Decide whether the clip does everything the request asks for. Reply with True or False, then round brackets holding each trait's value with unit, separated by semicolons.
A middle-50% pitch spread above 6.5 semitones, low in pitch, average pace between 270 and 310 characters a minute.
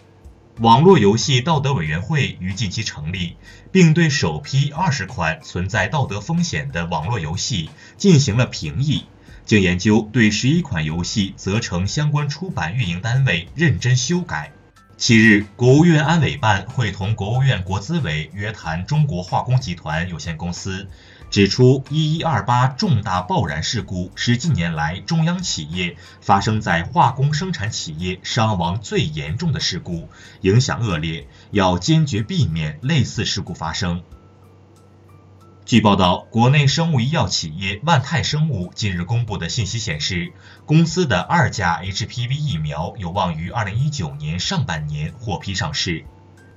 False (7.2 semitones; 110 Hz; 245 characters per minute)